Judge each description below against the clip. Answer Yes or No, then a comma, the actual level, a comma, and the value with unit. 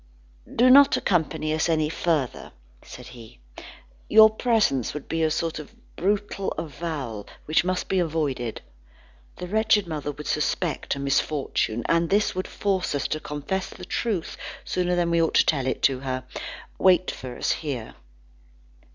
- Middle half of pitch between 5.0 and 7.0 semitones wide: No, average, 4.6 semitones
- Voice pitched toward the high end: No, medium, 160 Hz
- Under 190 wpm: Yes, average, 160 wpm